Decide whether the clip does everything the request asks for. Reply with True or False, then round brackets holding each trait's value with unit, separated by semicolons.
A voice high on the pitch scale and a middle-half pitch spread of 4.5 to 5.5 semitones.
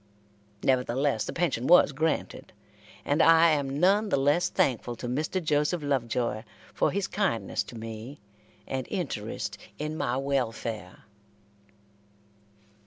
False (140 Hz; 4.8 semitones)